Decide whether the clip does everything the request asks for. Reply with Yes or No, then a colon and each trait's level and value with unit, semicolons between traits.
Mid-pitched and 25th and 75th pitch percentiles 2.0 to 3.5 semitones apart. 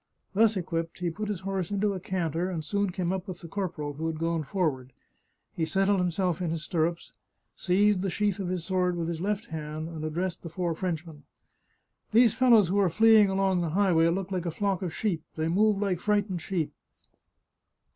Yes: medium, 180 Hz; average, 3.1 semitones